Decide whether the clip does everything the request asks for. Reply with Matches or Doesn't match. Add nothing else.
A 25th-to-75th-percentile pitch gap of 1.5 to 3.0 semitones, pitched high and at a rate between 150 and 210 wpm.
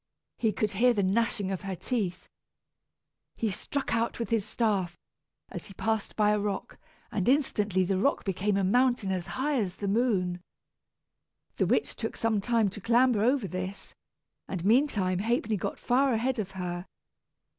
Doesn't match